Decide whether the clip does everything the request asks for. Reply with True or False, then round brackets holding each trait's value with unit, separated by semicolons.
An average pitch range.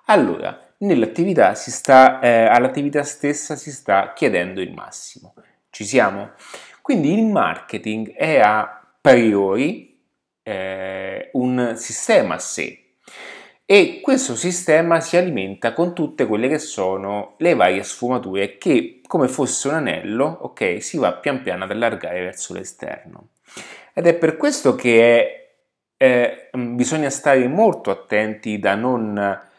False (6.8 semitones)